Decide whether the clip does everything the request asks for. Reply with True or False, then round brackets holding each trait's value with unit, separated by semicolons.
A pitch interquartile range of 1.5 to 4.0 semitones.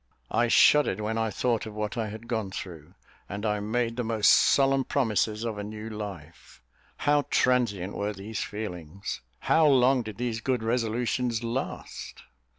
True (2.8 semitones)